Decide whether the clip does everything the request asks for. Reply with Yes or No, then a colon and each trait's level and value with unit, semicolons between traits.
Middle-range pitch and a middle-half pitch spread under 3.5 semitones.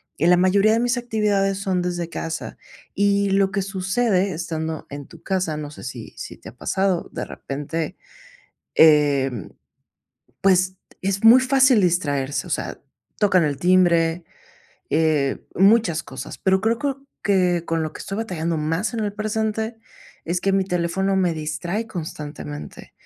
No: medium, 180 Hz; average, 4.0 semitones